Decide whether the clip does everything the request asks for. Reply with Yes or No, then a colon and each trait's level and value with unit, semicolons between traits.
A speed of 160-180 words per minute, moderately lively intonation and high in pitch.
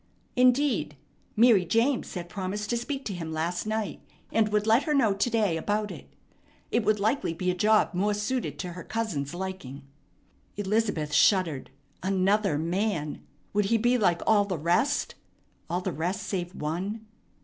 Yes: average, 165 wpm; average, 4.0 semitones; high, 200 Hz